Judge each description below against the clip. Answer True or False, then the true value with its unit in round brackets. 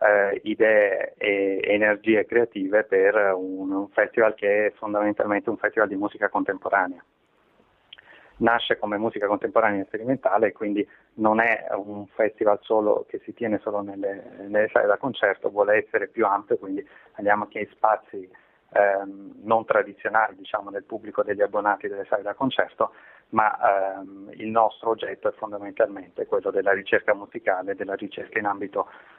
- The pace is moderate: True (150 wpm)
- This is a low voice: True (110 Hz)